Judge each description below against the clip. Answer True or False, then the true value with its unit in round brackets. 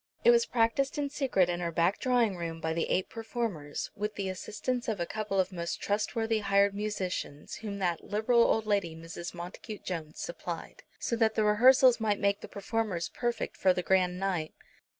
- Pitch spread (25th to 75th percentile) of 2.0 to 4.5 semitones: True (4.2 semitones)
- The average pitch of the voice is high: True (200 Hz)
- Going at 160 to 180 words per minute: False (190 wpm)